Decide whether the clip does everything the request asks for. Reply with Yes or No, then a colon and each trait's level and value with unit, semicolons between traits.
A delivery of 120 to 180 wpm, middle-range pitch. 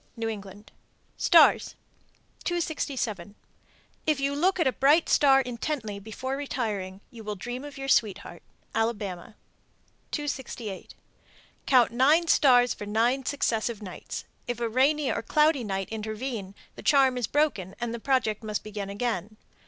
No: average, 145 wpm; high, 235 Hz